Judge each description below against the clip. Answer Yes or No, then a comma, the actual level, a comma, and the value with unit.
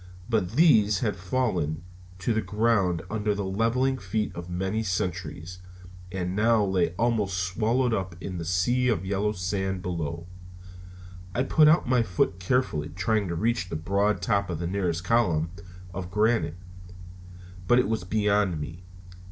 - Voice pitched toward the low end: Yes, very low, 95 Hz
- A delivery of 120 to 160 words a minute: Yes, average, 155 wpm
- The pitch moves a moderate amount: Yes, average, 3.8 semitones